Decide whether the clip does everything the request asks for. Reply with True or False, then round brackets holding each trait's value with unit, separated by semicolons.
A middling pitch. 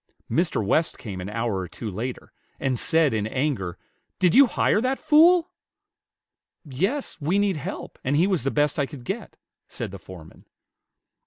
True (145 Hz)